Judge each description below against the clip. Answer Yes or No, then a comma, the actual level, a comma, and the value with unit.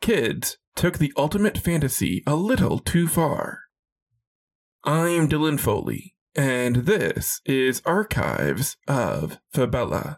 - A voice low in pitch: No, medium, 150 Hz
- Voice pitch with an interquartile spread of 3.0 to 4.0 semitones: No, average, 4.4 semitones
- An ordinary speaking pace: No, slow, 105 wpm